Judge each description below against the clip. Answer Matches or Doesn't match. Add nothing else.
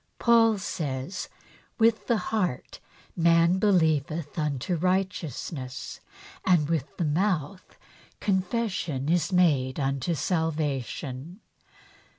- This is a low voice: Doesn't match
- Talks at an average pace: Doesn't match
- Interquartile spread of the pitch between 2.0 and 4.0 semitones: Doesn't match